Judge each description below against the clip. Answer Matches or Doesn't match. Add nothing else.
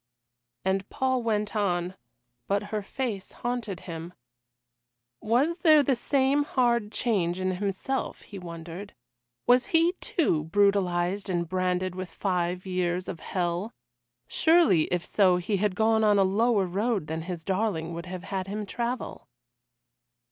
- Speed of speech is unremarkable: Matches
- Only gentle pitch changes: Doesn't match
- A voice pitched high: Matches